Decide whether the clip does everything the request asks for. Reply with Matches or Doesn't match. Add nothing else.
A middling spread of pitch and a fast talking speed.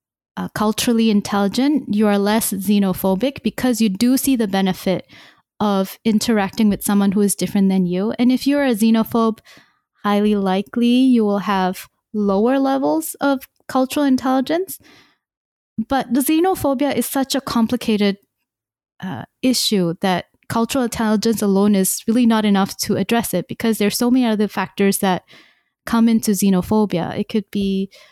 Doesn't match